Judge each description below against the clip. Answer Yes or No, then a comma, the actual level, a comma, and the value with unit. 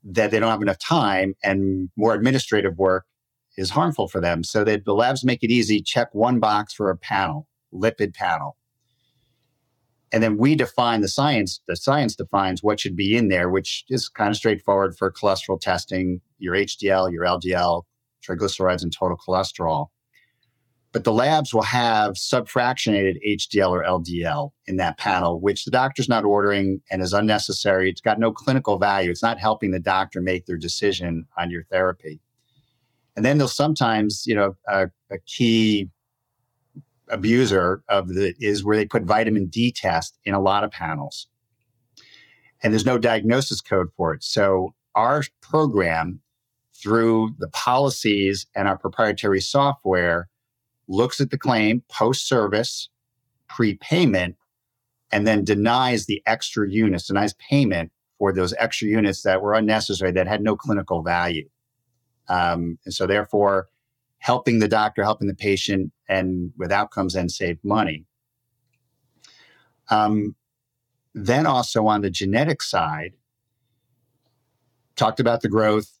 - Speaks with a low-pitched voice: Yes, low, 110 Hz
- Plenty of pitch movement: No, average, 4.3 semitones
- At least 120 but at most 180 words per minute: Yes, average, 150 wpm